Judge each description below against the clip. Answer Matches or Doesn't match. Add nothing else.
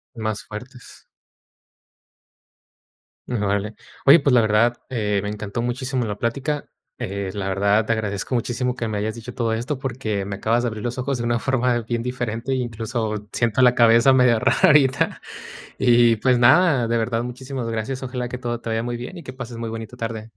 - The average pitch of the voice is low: Matches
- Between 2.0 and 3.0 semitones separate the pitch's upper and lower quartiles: Matches